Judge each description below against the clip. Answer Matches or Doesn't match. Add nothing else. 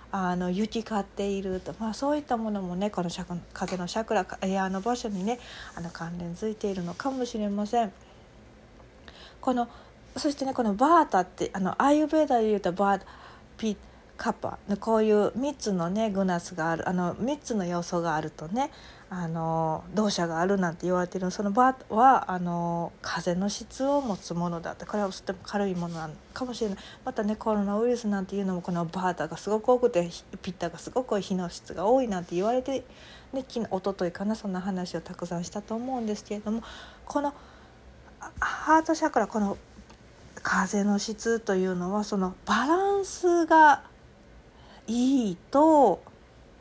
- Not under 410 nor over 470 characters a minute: Doesn't match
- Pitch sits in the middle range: Doesn't match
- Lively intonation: Doesn't match